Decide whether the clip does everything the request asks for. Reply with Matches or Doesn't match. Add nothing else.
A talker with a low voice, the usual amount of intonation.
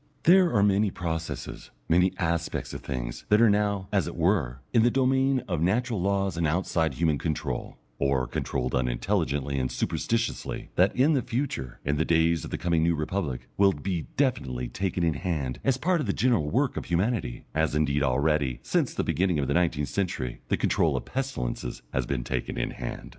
Doesn't match